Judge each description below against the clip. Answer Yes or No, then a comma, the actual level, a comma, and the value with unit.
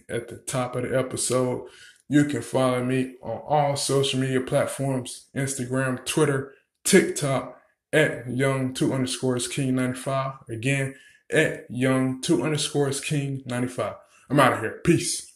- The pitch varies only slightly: Yes, narrow, 1.6 semitones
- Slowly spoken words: Yes, slow, 130 wpm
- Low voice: Yes, low, 130 Hz